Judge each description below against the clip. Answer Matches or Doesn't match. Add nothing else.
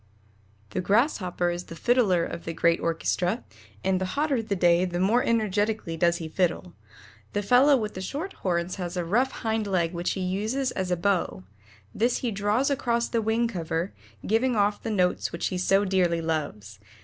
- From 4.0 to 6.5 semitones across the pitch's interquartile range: Matches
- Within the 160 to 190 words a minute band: Matches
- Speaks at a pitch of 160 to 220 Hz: Matches